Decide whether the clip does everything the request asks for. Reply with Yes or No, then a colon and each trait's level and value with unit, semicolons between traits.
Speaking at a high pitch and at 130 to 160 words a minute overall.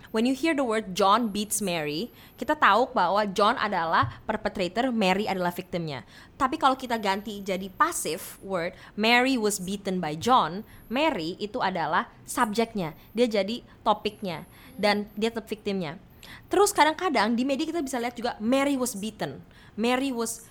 Yes: high, 215 Hz; average, 155 wpm